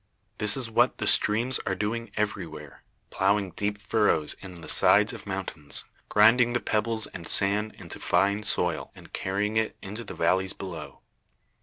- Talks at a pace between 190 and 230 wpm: No, average, 165 wpm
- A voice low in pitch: Yes, low, 105 Hz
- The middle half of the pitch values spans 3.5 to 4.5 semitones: No, average, 2.8 semitones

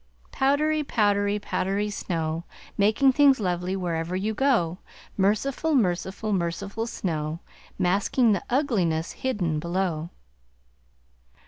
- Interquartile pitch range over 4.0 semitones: Yes, average, 5.1 semitones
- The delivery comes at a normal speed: No, slow, 100 wpm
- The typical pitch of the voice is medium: No, high, 200 Hz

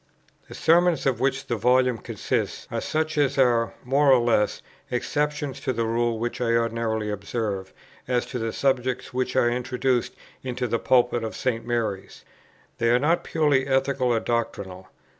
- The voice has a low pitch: Yes, low, 125 Hz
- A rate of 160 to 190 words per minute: Yes, average, 165 wpm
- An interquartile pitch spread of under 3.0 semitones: Yes, narrow, 2.5 semitones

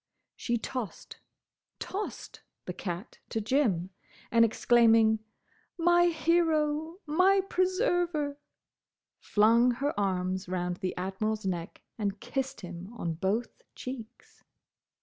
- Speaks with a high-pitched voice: Yes, high, 230 Hz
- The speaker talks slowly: Yes, slow, 95 wpm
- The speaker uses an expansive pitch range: Yes, wide, 8.0 semitones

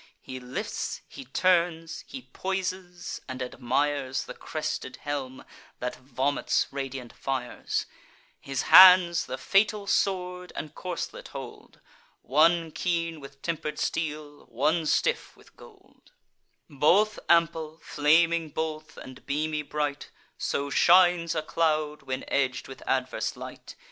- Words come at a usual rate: No, slow, 120 wpm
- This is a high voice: No, medium, 155 Hz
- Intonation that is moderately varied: Yes, average, 3.8 semitones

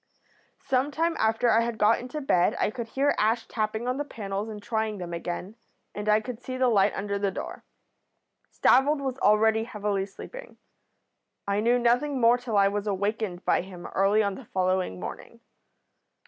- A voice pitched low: No, high, 220 Hz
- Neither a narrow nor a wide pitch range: Yes, average, 3.6 semitones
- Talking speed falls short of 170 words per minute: No, average, 180 wpm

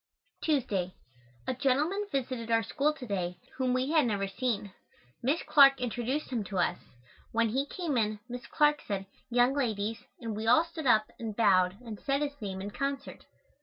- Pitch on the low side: No, high, 245 Hz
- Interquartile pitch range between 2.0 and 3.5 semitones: No, average, 4.8 semitones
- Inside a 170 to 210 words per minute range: Yes, average, 180 wpm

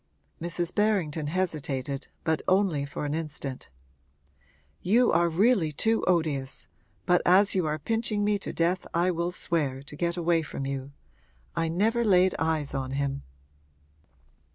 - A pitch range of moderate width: Yes, average, 4.3 semitones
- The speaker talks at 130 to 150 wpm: Yes, average, 145 wpm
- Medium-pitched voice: Yes, medium, 165 Hz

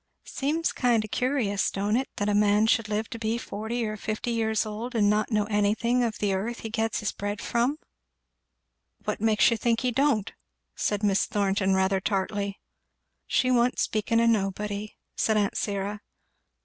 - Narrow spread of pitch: Yes, narrow, 2.3 semitones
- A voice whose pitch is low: No, high, 215 Hz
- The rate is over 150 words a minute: Yes, average, 180 wpm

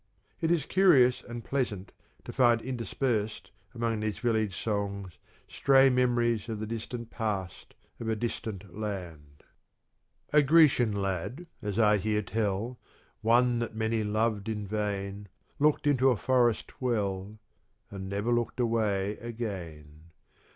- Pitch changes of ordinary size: Yes, average, 3.2 semitones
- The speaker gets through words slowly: Yes, slow, 130 wpm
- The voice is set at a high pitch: No, low, 110 Hz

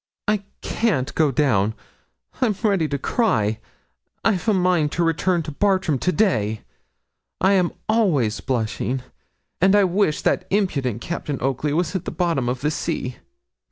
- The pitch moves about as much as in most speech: No, wide, 6.6 semitones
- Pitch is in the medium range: Yes, medium, 160 Hz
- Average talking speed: Yes, average, 155 wpm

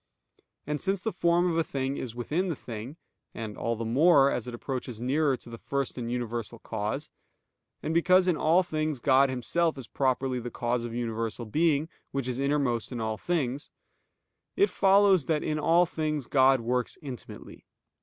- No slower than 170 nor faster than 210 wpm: Yes, average, 180 wpm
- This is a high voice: No, low, 135 Hz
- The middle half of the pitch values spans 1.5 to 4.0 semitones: No, average, 4.8 semitones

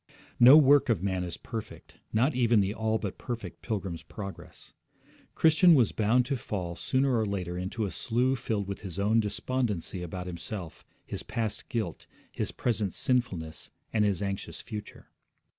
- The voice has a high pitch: No, low, 105 Hz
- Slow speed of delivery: No, average, 160 wpm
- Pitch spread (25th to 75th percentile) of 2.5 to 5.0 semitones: Yes, average, 4.2 semitones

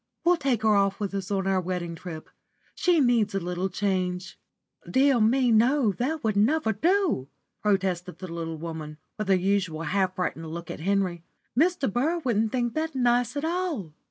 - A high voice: Yes, high, 200 Hz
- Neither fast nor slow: Yes, average, 180 wpm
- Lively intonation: Yes, wide, 6.0 semitones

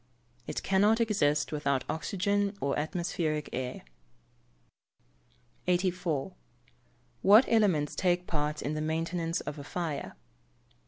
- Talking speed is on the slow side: Yes, slow, 105 wpm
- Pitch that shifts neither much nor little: Yes, average, 4.2 semitones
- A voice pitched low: No, medium, 165 Hz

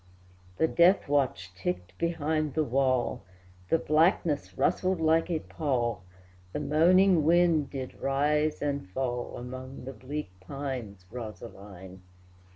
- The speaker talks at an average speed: No, slow, 120 wpm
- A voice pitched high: No, medium, 140 Hz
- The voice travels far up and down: No, average, 4.8 semitones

